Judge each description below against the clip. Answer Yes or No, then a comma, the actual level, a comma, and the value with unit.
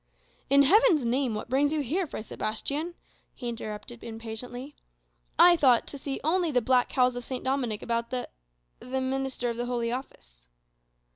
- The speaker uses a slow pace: No, average, 165 wpm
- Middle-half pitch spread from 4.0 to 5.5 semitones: No, average, 3.2 semitones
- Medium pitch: No, very high, 255 Hz